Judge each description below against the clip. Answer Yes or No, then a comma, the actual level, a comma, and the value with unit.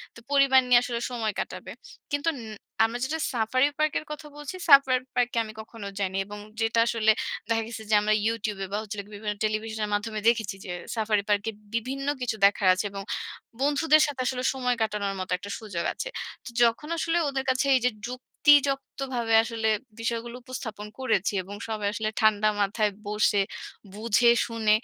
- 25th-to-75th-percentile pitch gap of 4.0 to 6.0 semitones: No, average, 3.4 semitones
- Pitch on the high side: Yes, high, 230 Hz